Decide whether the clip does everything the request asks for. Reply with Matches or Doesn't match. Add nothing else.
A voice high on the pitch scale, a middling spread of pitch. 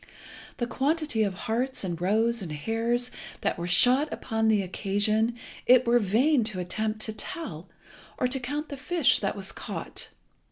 Matches